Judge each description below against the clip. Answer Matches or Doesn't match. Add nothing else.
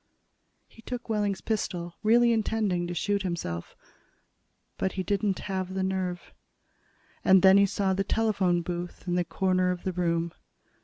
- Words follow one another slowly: Doesn't match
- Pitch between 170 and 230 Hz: Matches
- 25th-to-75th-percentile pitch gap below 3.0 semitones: Matches